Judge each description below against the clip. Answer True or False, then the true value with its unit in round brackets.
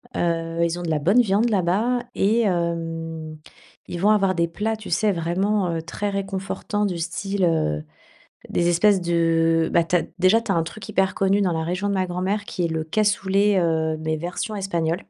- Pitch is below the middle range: False (180 Hz)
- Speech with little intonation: False (3.4 semitones)